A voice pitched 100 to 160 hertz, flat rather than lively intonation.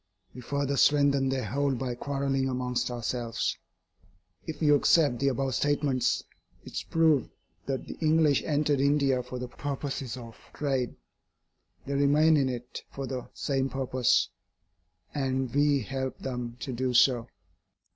Yes: low, 135 Hz; narrow, 2.2 semitones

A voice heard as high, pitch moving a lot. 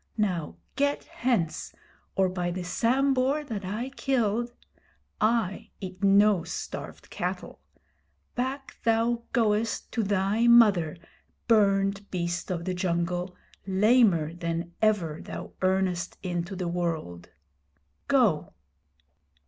No: high, 195 Hz; average, 4.6 semitones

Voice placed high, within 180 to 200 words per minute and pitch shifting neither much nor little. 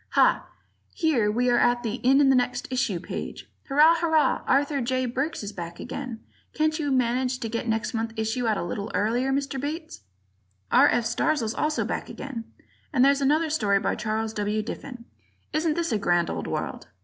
Yes: very high, 250 Hz; average, 195 wpm; average, 4.3 semitones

